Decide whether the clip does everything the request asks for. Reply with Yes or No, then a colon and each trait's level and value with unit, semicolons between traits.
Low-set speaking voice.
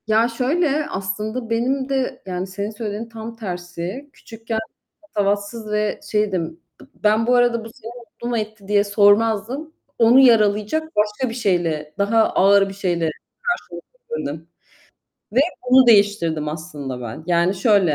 No: high, 210 Hz